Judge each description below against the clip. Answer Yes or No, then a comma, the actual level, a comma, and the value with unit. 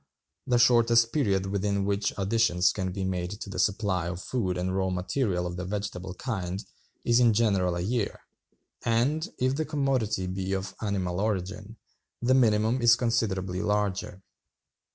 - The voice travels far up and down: No, average, 3.8 semitones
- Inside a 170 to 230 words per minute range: No, average, 155 wpm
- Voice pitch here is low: Yes, low, 100 Hz